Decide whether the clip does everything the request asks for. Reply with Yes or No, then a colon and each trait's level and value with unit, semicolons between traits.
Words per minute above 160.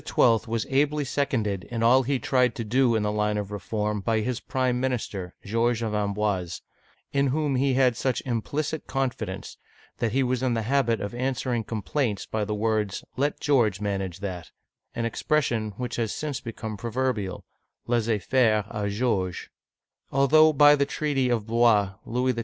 Yes: average, 170 wpm